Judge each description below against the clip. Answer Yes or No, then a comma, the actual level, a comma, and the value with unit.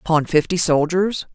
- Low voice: No, medium, 170 Hz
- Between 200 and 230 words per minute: No, slow, 135 wpm